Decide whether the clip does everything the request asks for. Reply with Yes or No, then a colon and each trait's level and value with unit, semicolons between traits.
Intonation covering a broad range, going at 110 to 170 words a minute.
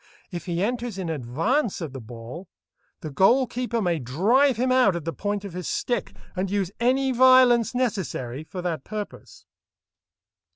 Yes: wide, 6.7 semitones; average, 165 wpm